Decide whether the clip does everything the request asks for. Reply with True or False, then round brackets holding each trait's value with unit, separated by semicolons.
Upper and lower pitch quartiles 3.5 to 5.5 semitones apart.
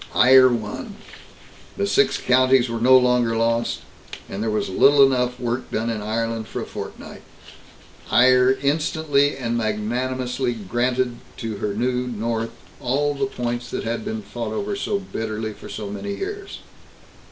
False (2.5 semitones)